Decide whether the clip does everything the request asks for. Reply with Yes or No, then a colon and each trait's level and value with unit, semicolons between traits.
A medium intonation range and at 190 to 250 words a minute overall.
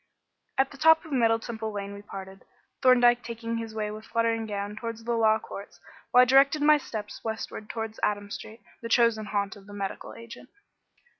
No: narrow, 2.3 semitones; average, 195 wpm